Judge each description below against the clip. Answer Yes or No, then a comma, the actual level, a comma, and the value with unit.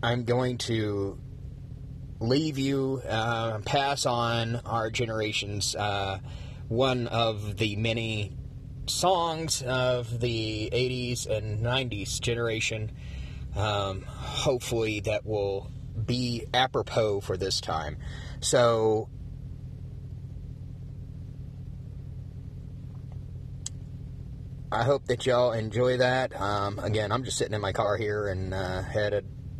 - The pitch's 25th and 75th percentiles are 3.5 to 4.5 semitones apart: No, average, 2.8 semitones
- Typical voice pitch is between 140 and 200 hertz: No, low, 120 Hz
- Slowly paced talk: Yes, slow, 100 wpm